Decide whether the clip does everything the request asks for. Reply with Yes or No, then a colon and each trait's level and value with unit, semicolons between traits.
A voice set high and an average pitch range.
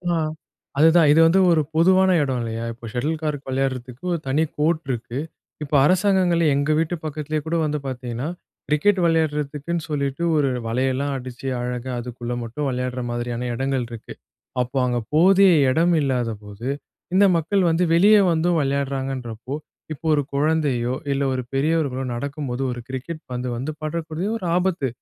No: medium, 140 Hz; average, 4.3 semitones